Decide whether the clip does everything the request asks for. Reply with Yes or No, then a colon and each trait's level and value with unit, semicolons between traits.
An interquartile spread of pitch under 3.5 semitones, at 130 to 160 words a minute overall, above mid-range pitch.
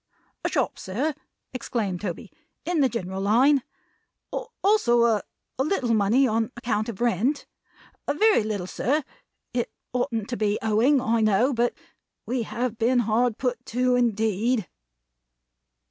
Yes: average, 2.9 semitones; average, 145 wpm; high, 235 Hz